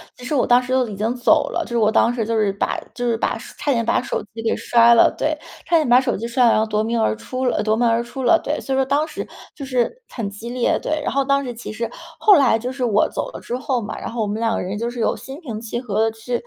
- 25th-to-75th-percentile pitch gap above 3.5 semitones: No, average, 2.8 semitones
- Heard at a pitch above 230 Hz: Yes, high, 240 Hz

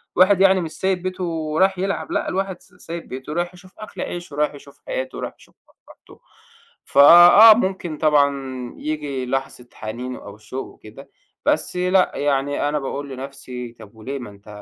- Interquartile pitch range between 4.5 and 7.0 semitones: Yes, average, 5.3 semitones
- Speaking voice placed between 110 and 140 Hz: No, medium, 150 Hz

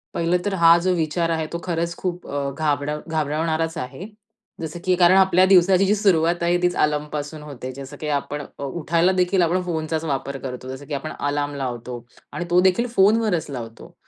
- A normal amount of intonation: Yes, average, 3.6 semitones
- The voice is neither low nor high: Yes, medium, 160 Hz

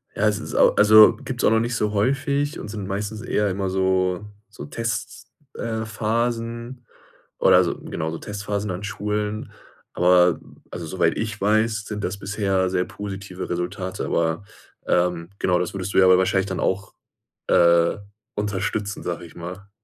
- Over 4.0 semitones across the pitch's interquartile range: No, average, 2.8 semitones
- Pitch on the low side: Yes, low, 100 Hz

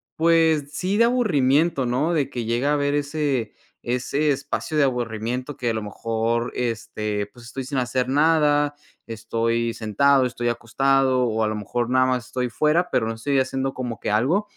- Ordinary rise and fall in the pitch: Yes, average, 3.8 semitones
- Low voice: Yes, low, 130 Hz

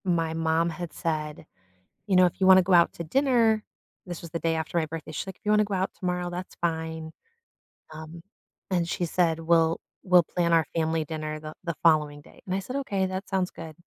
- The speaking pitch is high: No, medium, 170 Hz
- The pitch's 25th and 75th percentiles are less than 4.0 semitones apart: Yes, narrow, 2.5 semitones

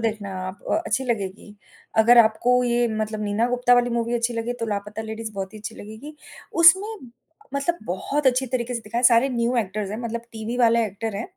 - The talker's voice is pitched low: No, high, 230 Hz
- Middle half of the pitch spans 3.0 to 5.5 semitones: No, narrow, 2.4 semitones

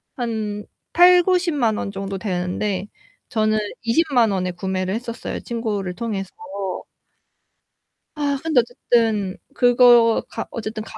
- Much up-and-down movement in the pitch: No, average, 3.7 semitones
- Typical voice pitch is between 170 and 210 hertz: No, high, 225 Hz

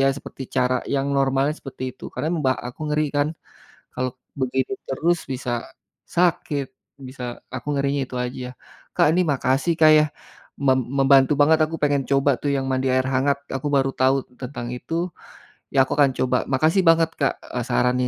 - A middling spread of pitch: No, narrow, 2.3 semitones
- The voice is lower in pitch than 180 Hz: Yes, low, 135 Hz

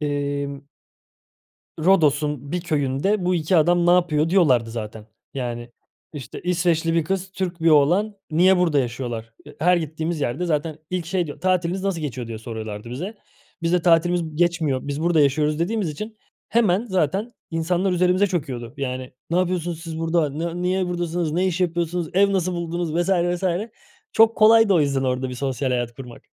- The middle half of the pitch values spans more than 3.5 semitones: Yes, average, 4.1 semitones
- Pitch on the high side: No, medium, 165 Hz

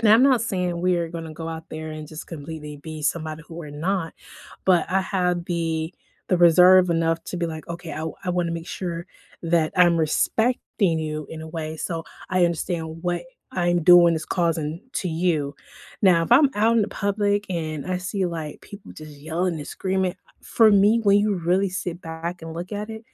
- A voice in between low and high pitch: Yes, medium, 170 Hz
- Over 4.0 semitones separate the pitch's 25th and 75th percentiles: No, narrow, 2.5 semitones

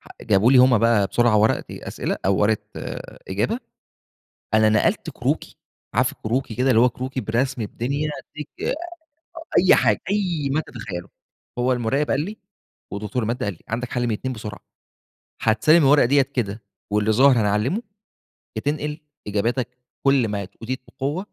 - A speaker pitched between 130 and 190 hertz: No, low, 120 Hz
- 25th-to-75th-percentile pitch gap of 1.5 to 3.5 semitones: No, average, 4.1 semitones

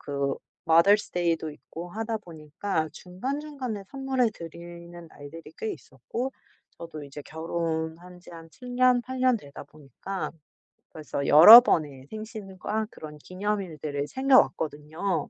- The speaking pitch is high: No, medium, 175 Hz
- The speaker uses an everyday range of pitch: No, wide, 5.7 semitones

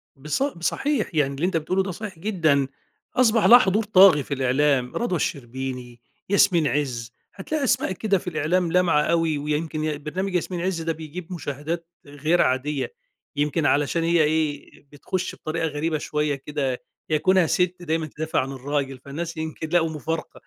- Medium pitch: Yes, medium, 160 Hz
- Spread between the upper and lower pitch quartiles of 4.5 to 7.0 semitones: No, average, 3.8 semitones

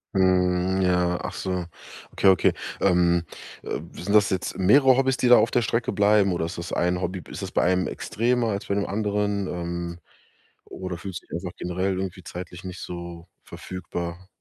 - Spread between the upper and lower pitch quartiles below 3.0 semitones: Yes, narrow, 2.4 semitones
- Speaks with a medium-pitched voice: No, very low, 95 Hz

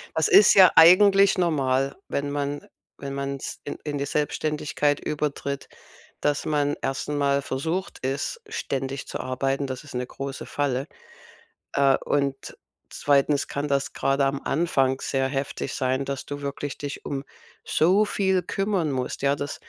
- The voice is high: No, medium, 140 Hz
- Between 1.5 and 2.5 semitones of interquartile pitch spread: Yes, narrow, 1.8 semitones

